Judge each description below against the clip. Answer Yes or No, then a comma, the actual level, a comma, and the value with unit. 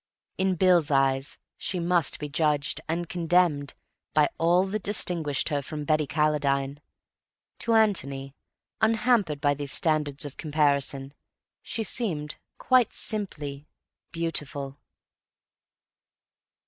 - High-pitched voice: No, medium, 155 Hz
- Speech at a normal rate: No, slow, 110 wpm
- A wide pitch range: No, average, 3.9 semitones